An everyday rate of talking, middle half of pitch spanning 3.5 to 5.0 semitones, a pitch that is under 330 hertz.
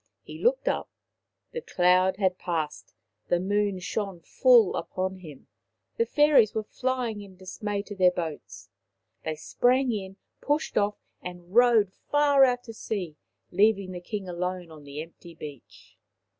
Yes: average, 150 wpm; average, 4.3 semitones; high, 190 Hz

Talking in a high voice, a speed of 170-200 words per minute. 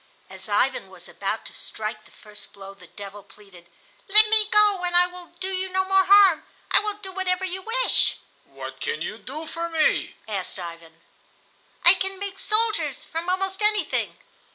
Yes: very high, 370 Hz; average, 180 wpm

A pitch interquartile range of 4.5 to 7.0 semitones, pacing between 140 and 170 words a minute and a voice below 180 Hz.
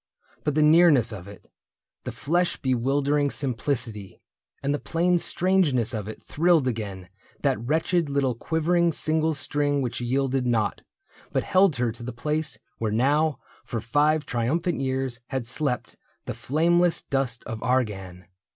Yes: average, 4.8 semitones; average, 145 wpm; low, 135 Hz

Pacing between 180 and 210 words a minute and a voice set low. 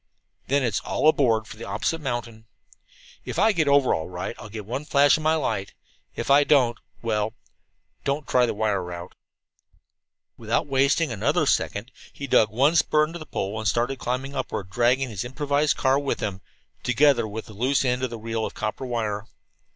Yes: average, 190 wpm; low, 125 Hz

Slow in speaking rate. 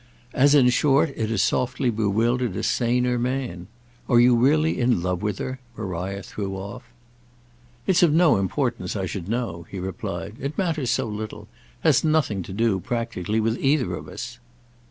No: average, 165 wpm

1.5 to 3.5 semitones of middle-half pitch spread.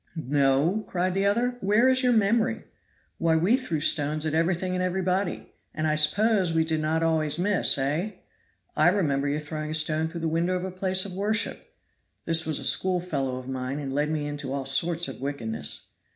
No: average, 4.1 semitones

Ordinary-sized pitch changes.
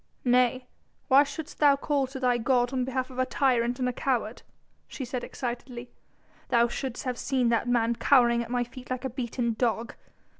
No: narrow, 1.6 semitones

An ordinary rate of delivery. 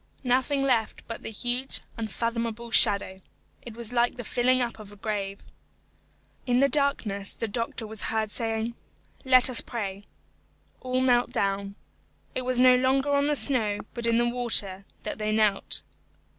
Yes: average, 160 wpm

